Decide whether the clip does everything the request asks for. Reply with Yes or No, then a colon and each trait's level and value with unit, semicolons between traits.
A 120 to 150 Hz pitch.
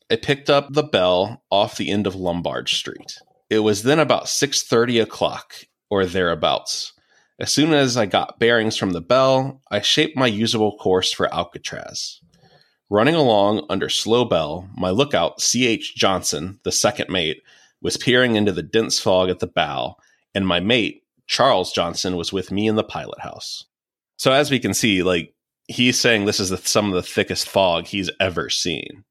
No: low, 110 Hz